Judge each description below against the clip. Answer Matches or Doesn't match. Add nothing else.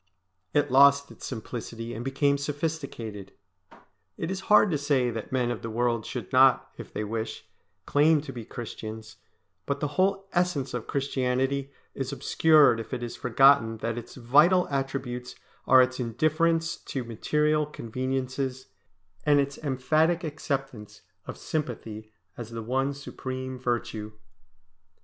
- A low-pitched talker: Matches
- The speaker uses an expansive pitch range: Doesn't match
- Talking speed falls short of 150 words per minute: Matches